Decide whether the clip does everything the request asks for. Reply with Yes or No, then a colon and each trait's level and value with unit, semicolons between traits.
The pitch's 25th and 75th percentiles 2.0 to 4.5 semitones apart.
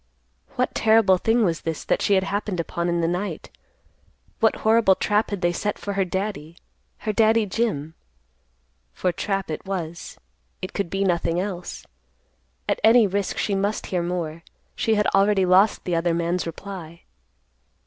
Yes: average, 3.3 semitones